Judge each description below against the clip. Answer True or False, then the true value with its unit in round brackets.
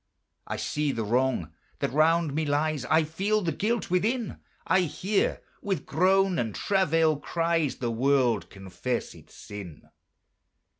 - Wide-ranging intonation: True (6.3 semitones)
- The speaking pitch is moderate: True (155 Hz)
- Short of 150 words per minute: True (140 wpm)